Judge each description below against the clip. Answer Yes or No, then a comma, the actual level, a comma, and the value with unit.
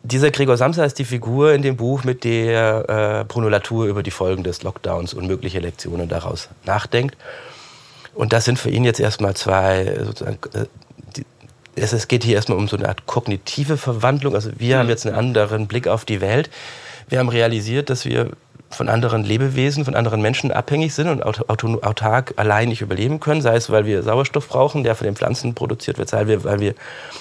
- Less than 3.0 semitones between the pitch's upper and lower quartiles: No, average, 3.5 semitones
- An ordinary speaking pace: No, fast, 195 wpm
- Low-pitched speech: Yes, low, 115 Hz